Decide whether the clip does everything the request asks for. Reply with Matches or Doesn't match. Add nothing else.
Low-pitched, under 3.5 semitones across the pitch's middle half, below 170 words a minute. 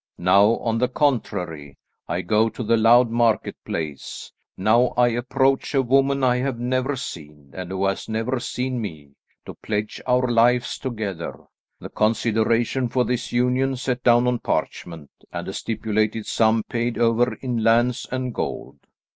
Matches